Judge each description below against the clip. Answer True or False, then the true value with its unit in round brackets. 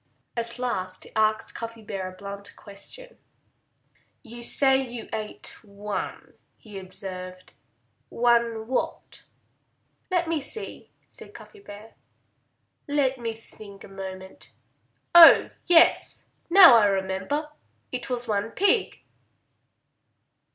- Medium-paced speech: False (110 wpm)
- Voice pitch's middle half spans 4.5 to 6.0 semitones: True (4.9 semitones)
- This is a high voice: True (225 Hz)